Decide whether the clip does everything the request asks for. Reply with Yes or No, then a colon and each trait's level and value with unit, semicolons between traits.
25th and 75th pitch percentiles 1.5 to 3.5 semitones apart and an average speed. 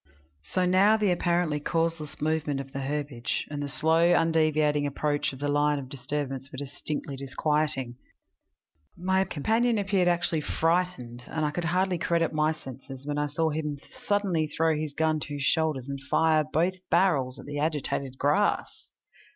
Yes: average, 2.9 semitones; average, 165 wpm